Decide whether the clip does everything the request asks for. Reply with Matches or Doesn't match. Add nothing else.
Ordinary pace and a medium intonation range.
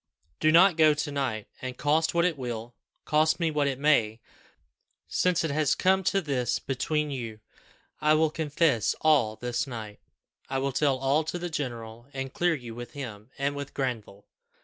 Matches